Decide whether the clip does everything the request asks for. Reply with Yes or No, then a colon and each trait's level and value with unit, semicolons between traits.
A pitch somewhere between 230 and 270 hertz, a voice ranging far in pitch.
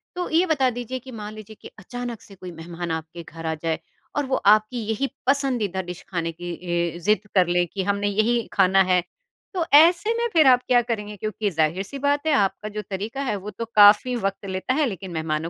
No: high, 210 Hz; wide, 5.8 semitones